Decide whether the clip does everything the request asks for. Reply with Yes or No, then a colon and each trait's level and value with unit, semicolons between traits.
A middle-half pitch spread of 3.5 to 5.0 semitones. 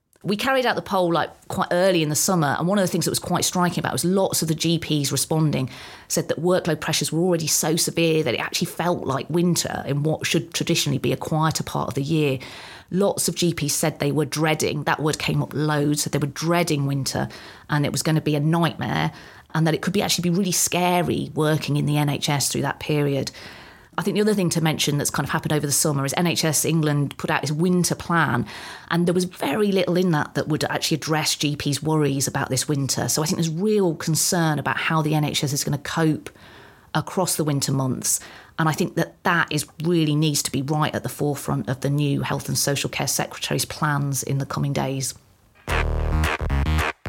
No: average, 3.1 semitones